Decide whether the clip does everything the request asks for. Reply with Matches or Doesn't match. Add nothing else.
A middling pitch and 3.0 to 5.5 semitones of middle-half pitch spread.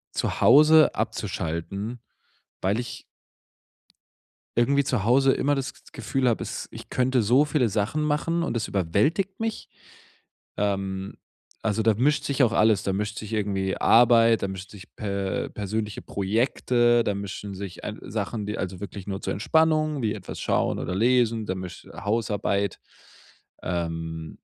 Doesn't match